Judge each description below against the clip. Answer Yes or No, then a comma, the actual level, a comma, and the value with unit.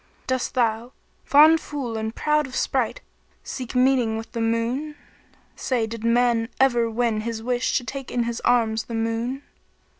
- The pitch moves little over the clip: Yes, narrow, 2.3 semitones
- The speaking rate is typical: Yes, average, 160 wpm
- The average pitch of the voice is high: Yes, high, 240 Hz